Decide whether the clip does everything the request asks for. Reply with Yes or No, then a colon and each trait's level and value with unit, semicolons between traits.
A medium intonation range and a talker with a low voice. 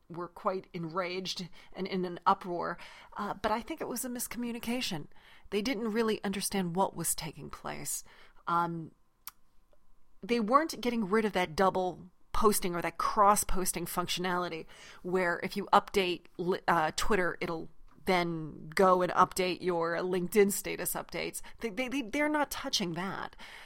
No: average, 3.7 semitones; high, 190 Hz